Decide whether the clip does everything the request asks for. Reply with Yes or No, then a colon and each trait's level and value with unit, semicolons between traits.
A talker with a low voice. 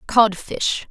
No: high, 210 Hz